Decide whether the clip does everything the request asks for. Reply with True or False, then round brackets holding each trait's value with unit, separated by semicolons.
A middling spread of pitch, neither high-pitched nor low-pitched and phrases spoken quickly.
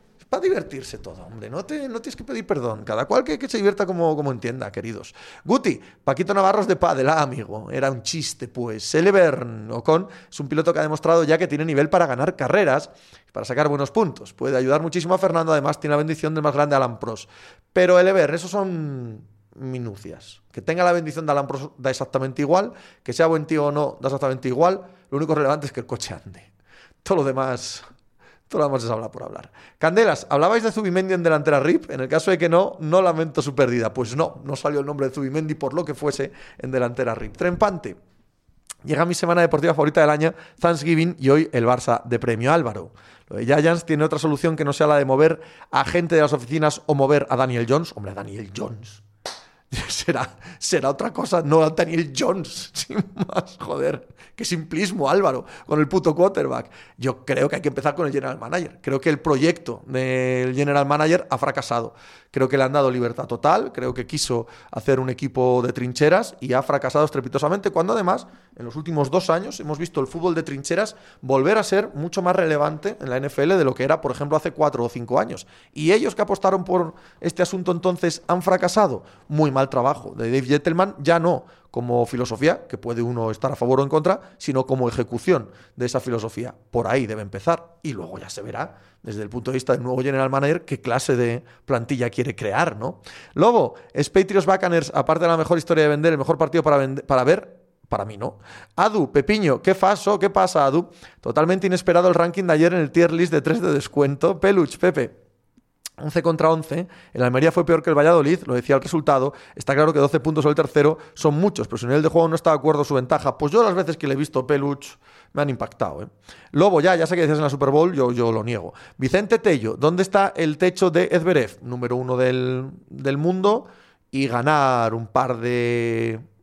True (4.9 semitones; 150 Hz; 215 wpm)